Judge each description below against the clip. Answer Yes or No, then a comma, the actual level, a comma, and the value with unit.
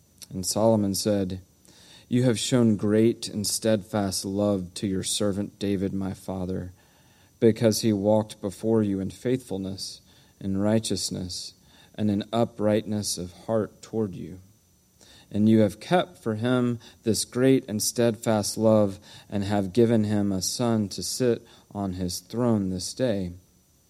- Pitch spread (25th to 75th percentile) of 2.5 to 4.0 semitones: Yes, average, 3.0 semitones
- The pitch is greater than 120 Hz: No, low, 105 Hz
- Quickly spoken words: No, average, 140 wpm